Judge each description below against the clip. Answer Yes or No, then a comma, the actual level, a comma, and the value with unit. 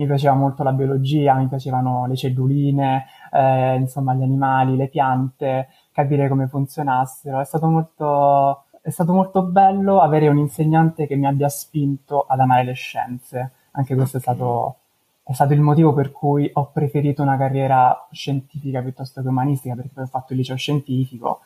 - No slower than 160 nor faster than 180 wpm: Yes, fast, 170 wpm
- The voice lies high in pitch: No, low, 135 Hz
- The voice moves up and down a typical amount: No, narrow, 1.9 semitones